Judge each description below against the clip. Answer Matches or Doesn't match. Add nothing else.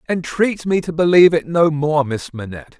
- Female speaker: Doesn't match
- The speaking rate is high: Doesn't match